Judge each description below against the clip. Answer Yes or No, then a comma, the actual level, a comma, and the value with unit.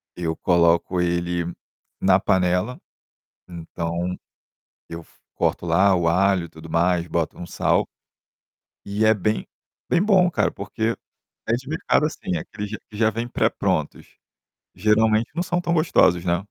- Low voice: Yes, very low, 95 Hz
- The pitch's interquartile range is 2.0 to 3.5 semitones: No, average, 4.3 semitones